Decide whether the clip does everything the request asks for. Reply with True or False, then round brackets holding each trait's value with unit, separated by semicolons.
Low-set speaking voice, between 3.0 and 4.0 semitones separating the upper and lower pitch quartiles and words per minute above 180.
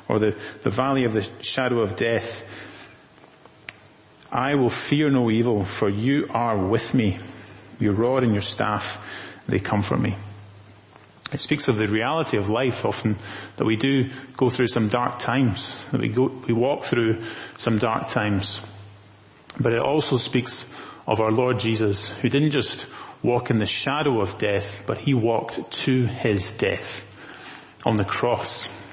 False (115 Hz; 3.5 semitones; 165 wpm)